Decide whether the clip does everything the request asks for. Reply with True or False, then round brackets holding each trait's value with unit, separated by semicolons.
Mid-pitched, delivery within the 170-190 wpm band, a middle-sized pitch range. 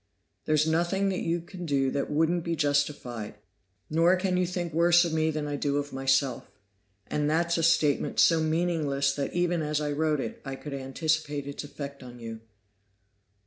True (155 Hz; 180 wpm; 3.2 semitones)